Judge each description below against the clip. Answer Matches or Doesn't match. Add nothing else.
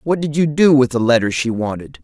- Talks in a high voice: Doesn't match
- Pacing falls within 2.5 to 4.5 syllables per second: Doesn't match